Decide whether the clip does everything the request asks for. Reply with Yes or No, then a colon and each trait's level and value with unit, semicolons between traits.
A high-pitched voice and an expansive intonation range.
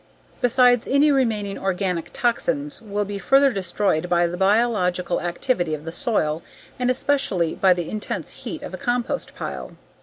Yes: high, 205 Hz; wide, 5.7 semitones